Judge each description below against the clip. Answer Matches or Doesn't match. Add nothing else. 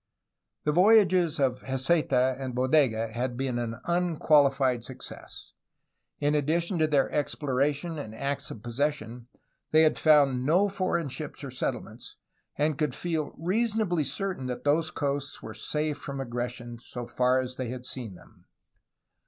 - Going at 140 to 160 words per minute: Matches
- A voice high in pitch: Doesn't match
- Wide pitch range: Doesn't match